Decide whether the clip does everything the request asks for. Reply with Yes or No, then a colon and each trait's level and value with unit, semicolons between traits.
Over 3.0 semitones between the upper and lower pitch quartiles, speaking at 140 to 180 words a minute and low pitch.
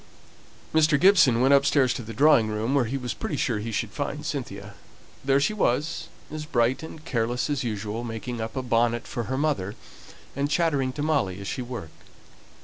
No: average, 4.1 semitones; average, 190 wpm; low, 130 Hz